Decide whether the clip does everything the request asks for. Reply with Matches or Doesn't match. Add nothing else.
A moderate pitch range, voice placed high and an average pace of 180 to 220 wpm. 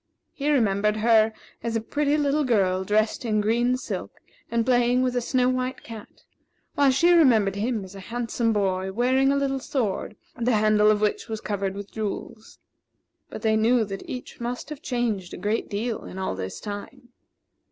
Matches